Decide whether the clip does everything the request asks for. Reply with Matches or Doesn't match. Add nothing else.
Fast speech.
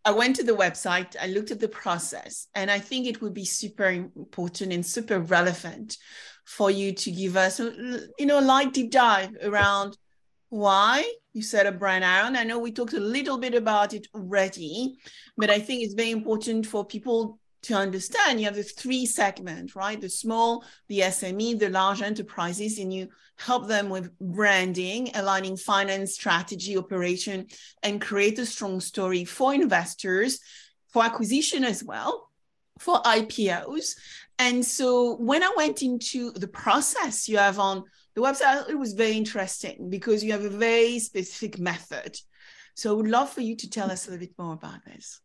Doesn't match